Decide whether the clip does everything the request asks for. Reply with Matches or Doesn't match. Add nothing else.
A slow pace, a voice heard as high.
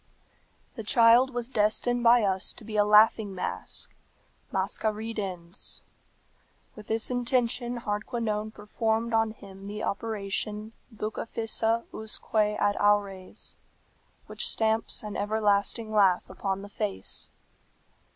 Matches